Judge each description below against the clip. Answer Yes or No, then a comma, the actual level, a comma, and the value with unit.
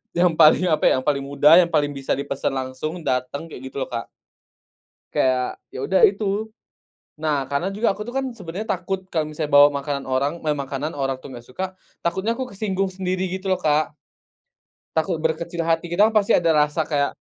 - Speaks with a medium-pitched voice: Yes, medium, 160 Hz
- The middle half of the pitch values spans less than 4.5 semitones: No, average, 5.0 semitones